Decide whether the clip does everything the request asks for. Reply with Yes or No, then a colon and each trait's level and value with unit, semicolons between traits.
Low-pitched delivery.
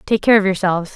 No: high, 195 Hz